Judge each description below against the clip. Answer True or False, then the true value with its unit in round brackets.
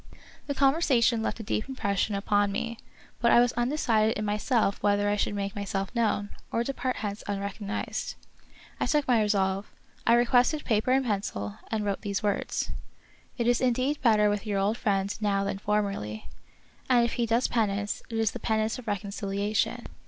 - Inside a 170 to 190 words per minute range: True (180 wpm)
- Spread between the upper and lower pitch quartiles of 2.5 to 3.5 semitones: True (2.9 semitones)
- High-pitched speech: True (215 Hz)